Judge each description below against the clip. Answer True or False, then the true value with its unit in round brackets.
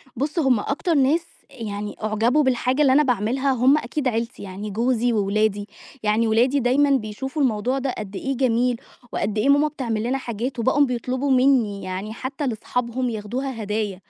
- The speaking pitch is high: True (245 Hz)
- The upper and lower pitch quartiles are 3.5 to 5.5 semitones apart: True (3.9 semitones)